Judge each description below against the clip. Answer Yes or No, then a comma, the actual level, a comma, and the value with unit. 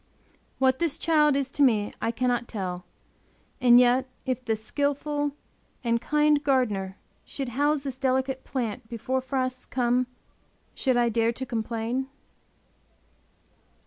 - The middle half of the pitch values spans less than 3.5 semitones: Yes, average, 2.8 semitones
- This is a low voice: No, very high, 255 Hz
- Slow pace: Yes, slow, 130 wpm